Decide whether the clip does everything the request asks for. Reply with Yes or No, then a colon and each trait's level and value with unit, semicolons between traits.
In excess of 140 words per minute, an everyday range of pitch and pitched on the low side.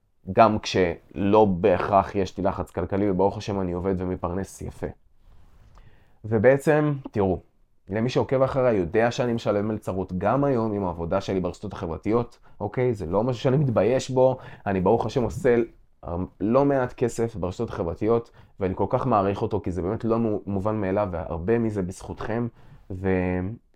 Yes: fast, 150 wpm; average, 4.0 semitones; low, 105 Hz